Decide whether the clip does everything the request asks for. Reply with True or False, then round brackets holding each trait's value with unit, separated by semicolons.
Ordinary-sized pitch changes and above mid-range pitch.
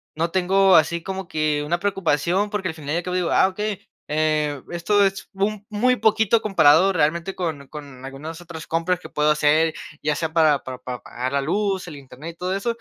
False (4.2 semitones; 170 Hz)